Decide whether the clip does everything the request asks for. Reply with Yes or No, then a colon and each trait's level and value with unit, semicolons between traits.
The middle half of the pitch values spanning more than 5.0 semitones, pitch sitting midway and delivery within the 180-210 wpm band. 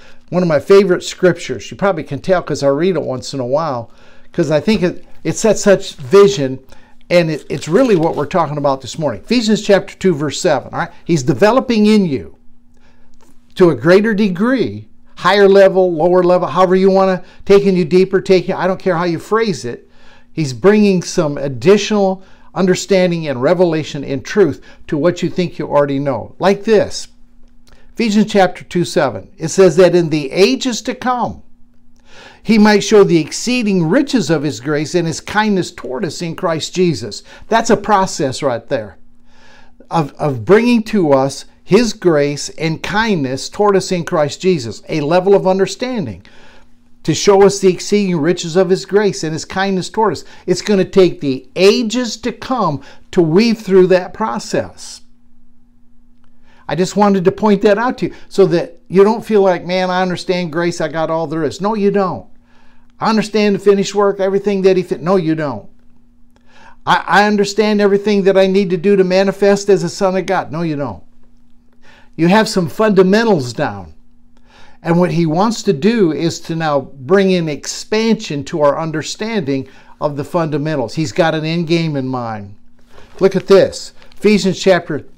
Yes: wide, 5.4 semitones; medium, 180 Hz; average, 185 wpm